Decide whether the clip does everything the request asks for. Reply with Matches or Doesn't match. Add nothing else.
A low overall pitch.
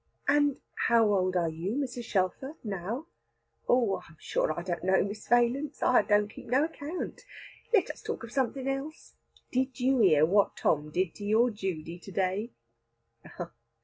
Doesn't match